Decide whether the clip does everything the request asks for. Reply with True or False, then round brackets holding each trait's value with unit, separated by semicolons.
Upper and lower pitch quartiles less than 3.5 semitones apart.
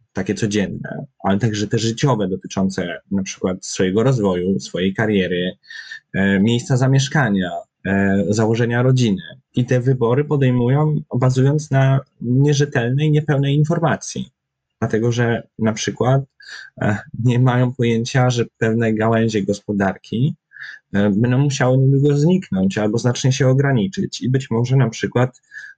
False (4.5 semitones)